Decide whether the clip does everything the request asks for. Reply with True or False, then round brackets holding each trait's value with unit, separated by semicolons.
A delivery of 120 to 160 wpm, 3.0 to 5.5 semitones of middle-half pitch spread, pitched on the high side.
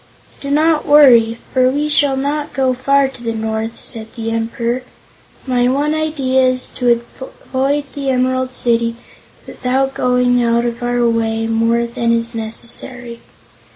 False (150 wpm; 2.6 semitones; 250 Hz)